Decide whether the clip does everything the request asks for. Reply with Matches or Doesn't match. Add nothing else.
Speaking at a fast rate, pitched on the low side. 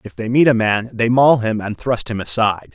Matches